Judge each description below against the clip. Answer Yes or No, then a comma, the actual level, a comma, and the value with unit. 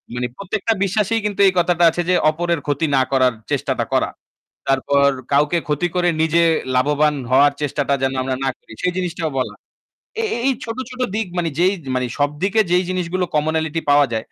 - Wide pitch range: No, average, 4.3 semitones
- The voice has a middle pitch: Yes, medium, 160 Hz